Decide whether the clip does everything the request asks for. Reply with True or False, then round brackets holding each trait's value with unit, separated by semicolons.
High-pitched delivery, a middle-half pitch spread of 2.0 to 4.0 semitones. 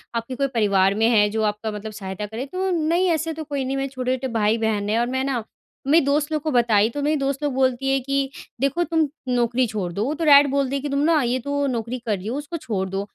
False (260 Hz; 4.4 semitones)